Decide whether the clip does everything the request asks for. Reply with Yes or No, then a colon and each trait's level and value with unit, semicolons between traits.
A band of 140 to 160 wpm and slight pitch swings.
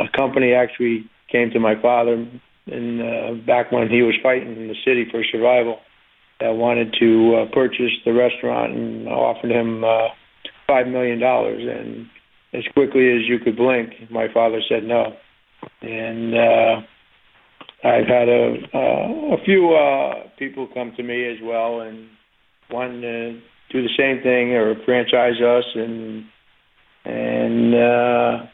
Yes: average, 150 wpm; narrow, 1.4 semitones